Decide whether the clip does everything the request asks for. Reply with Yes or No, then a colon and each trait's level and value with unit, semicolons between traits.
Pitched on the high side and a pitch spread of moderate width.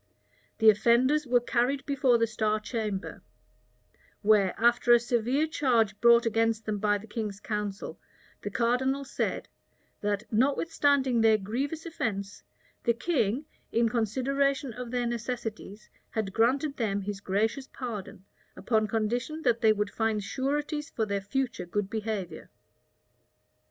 Yes: high, 230 Hz; average, 3.6 semitones